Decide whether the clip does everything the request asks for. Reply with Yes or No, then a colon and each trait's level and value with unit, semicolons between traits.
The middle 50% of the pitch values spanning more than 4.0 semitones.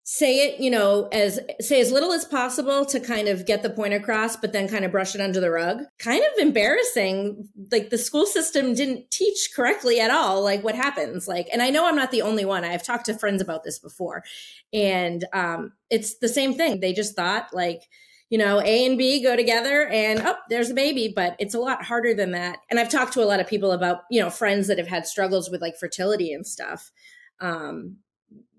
Yes: average, 4.7 semitones